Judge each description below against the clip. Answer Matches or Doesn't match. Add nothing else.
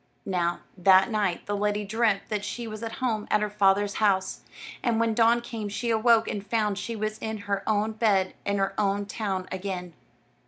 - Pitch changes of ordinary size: Doesn't match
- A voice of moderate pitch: Doesn't match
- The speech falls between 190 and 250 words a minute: Matches